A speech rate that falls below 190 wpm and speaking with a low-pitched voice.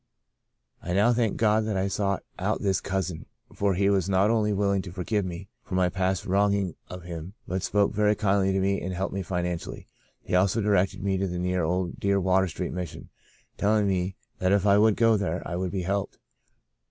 No: fast, 205 wpm; very low, 95 Hz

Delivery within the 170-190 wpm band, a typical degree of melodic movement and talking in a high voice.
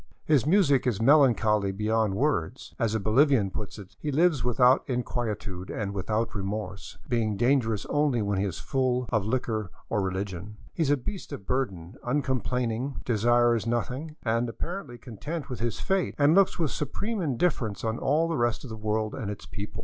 No: average, 180 wpm; average, 4.6 semitones; low, 120 Hz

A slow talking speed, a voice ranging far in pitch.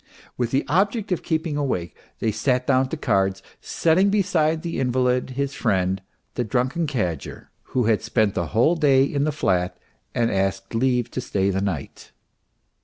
No: average, 175 wpm; wide, 7.1 semitones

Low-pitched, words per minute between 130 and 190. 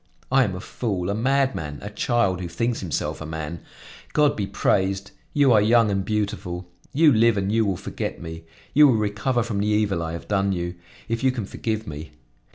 No: low, 105 Hz; fast, 205 wpm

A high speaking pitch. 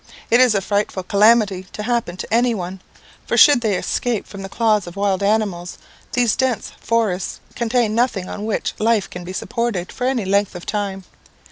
Yes: high, 210 Hz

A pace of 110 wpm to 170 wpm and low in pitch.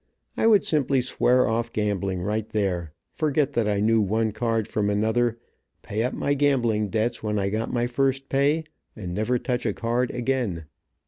No: average, 180 wpm; low, 115 Hz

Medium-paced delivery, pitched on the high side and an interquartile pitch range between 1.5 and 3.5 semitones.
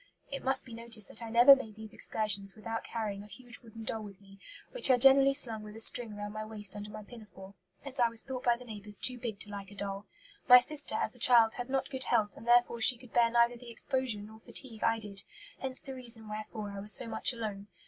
No: fast, 250 wpm; high, 225 Hz; average, 2.8 semitones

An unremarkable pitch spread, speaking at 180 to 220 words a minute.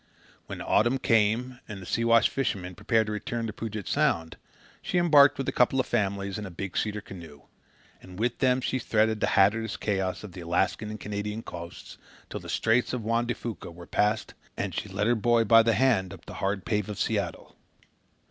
Yes: average, 3.2 semitones; fast, 205 wpm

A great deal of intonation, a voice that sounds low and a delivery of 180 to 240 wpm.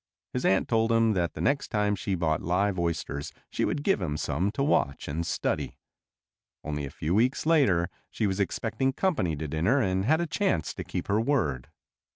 Yes: wide, 7.3 semitones; low, 100 Hz; average, 195 wpm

